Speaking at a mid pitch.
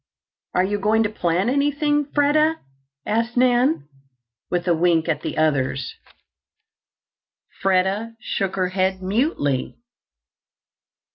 No: high, 195 Hz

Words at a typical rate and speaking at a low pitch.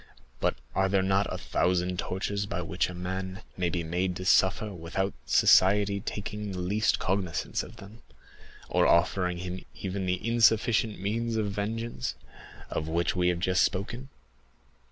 Yes: average, 155 wpm; very low, 95 Hz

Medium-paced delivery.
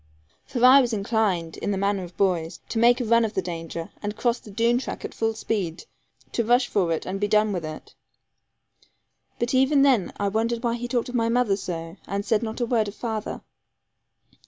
No: fast, 215 wpm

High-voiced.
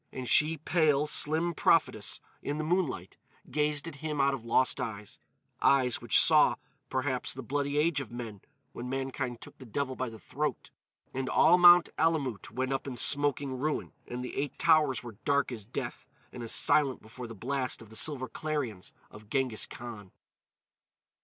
No: low, 135 Hz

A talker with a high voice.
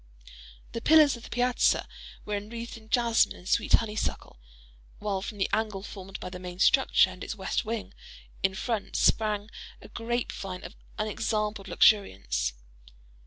Yes: high, 210 Hz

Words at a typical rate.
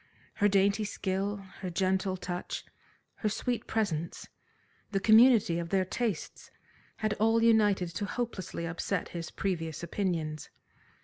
No: slow, 125 wpm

